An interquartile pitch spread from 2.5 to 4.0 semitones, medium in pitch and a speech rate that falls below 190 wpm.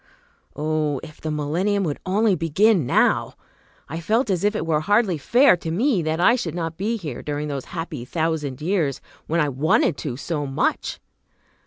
No: average, 4.8 semitones; medium, 165 Hz; average, 180 wpm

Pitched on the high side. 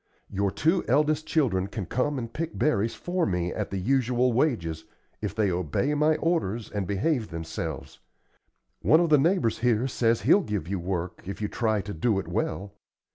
No: low, 115 Hz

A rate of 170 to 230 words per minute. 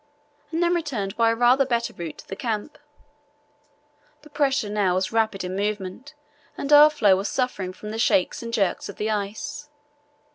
Yes: average, 180 wpm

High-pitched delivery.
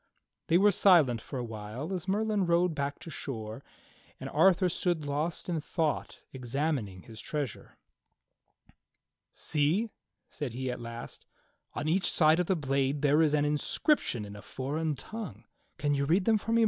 No: medium, 150 Hz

